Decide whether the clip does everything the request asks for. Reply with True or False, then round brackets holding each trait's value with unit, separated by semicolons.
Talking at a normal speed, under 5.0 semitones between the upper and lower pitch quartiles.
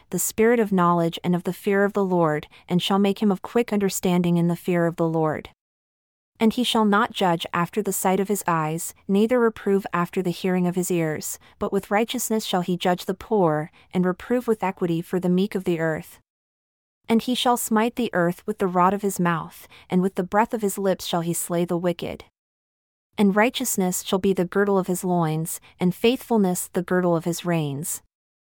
False (215 wpm; 2.9 semitones)